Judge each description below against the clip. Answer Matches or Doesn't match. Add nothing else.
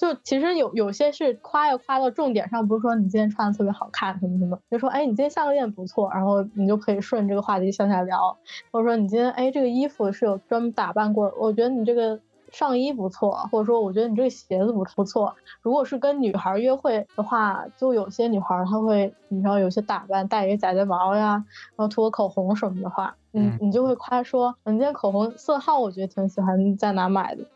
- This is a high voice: Matches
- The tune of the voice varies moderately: Matches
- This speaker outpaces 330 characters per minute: Matches